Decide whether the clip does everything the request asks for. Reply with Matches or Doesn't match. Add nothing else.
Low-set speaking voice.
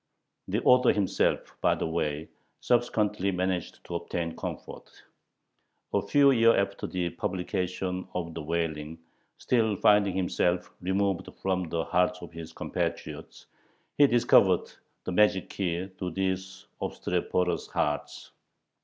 Matches